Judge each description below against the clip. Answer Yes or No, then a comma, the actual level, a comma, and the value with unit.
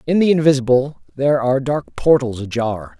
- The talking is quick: No, average, 160 wpm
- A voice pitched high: No, low, 135 Hz